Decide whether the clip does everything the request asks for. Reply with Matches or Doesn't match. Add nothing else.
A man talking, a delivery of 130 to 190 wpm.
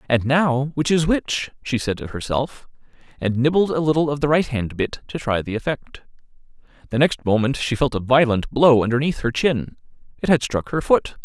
Doesn't match